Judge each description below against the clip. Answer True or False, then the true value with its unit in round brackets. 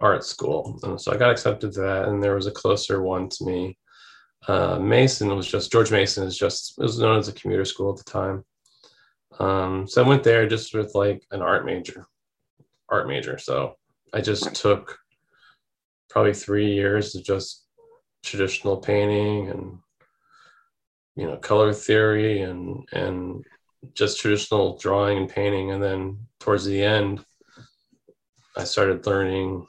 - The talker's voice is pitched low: True (100 Hz)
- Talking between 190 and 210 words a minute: False (160 wpm)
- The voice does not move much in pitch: True (1.7 semitones)